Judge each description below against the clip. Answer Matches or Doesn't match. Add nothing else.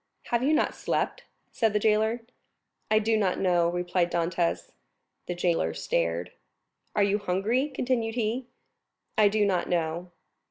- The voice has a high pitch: Matches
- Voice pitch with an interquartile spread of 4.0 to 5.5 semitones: Matches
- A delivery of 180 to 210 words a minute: Doesn't match